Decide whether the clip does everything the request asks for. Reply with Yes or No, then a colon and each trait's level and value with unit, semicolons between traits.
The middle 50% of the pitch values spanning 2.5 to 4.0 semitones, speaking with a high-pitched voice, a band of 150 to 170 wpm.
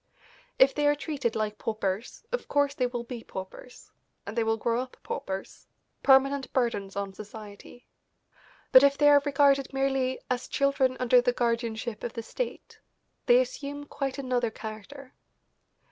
Yes: average, 3.7 semitones; very high, 250 Hz; average, 155 wpm